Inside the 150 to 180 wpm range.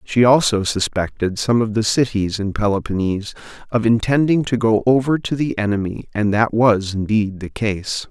Yes: average, 170 wpm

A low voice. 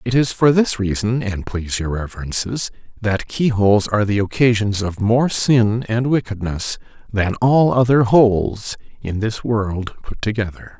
Yes: low, 110 Hz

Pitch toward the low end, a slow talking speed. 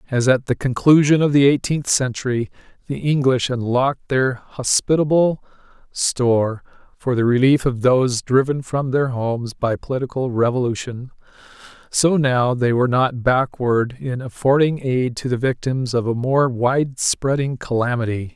No: low, 130 Hz; average, 145 wpm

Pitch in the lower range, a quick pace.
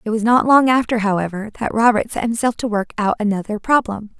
No: high, 220 Hz; fast, 215 wpm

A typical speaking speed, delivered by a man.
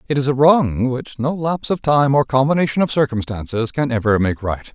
No: fast, 215 wpm; male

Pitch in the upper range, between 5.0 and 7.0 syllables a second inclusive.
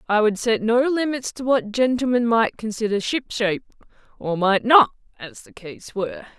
Yes: high, 225 Hz; 5.1 syllables/s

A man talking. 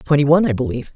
No: female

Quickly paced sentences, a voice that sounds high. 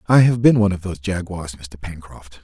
No: fast, 220 wpm; very low, 95 Hz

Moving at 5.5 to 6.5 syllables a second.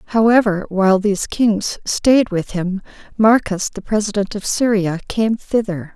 No: 4.3 syllables/s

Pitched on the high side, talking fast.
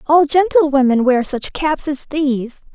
No: very high, 285 Hz; average, 155 wpm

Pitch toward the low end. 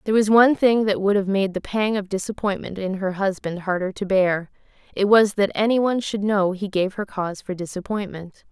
No: high, 200 Hz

